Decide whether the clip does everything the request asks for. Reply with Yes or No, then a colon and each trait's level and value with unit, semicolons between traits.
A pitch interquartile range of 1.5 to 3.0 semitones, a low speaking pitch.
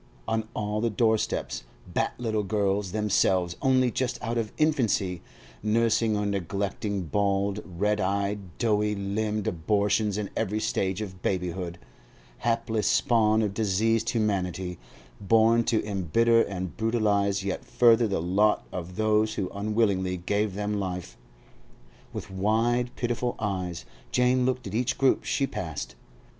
Yes: average, 2.7 semitones; low, 105 Hz